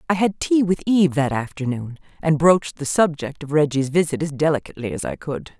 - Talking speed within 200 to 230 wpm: Yes, fast, 205 wpm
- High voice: No, medium, 155 Hz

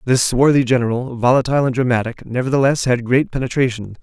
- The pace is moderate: Yes, average, 150 wpm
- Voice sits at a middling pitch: No, low, 125 Hz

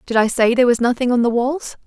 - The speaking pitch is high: Yes, high, 245 Hz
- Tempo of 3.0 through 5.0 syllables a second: No, 6.5 syllables/s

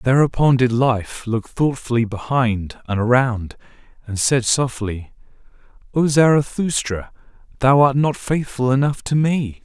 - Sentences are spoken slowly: Yes, slow, 125 wpm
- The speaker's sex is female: No, male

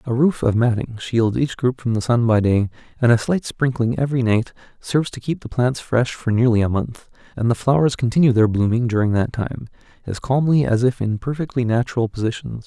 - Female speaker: No, male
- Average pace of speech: No, fast, 215 wpm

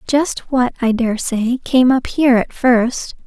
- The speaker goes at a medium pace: Yes, average, 185 wpm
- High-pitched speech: Yes, high, 245 Hz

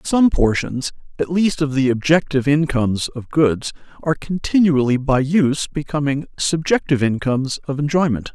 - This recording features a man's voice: Yes, male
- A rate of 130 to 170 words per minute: Yes, slow, 135 wpm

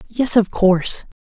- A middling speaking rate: Yes, average, 145 wpm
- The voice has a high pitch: Yes, high, 205 Hz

